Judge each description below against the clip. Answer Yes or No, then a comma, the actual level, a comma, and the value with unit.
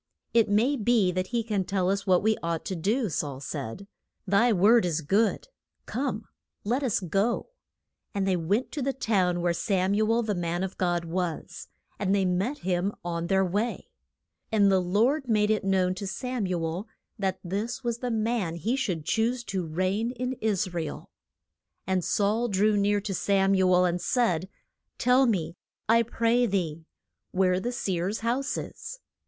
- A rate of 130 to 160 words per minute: No, average, 180 wpm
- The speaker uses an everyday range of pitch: Yes, average, 4.1 semitones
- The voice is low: No, high, 200 Hz